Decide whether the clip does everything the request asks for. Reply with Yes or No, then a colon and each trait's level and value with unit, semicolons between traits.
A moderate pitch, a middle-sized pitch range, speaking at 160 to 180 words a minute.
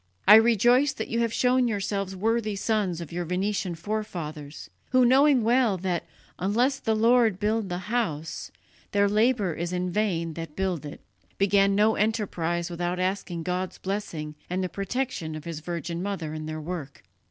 No: high, 195 Hz; average, 4.4 semitones; average, 165 wpm